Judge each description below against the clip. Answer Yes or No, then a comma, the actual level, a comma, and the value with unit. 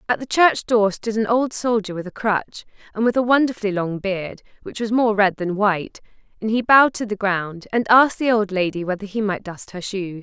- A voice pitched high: Yes, high, 210 Hz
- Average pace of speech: No, fast, 235 wpm